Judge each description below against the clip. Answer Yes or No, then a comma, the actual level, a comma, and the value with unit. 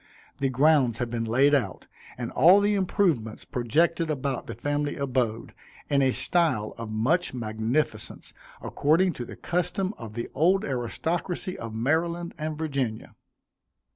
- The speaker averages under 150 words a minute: Yes, average, 140 wpm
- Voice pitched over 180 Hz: No, medium, 140 Hz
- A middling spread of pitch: No, wide, 6.1 semitones